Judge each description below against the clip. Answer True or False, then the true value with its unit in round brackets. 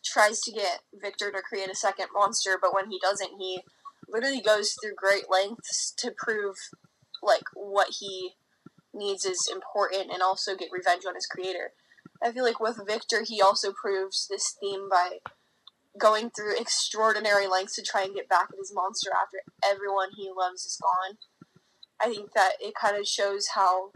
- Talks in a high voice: True (200 Hz)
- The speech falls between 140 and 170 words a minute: False (180 wpm)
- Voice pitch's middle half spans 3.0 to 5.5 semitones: False (2.4 semitones)